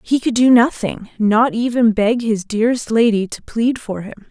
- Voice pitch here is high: Yes, high, 225 Hz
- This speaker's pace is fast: No, average, 180 wpm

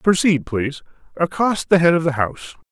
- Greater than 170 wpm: No, average, 155 wpm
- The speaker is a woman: No, male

